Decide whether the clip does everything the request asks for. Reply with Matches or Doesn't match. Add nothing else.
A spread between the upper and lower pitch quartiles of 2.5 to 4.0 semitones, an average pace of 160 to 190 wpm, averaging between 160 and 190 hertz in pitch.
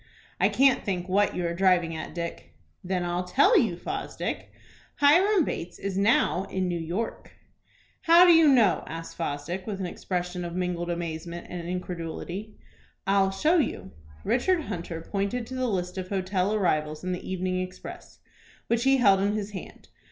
Matches